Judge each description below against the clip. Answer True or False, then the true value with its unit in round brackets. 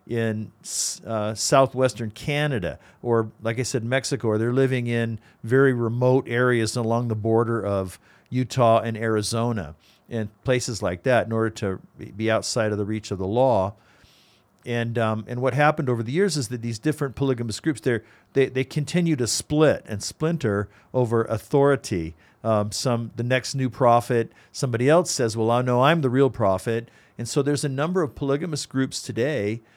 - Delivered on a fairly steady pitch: False (3.3 semitones)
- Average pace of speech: True (175 wpm)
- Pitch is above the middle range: False (120 Hz)